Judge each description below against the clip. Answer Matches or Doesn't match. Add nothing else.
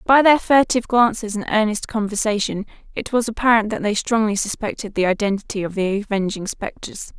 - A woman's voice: Matches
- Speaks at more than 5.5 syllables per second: Matches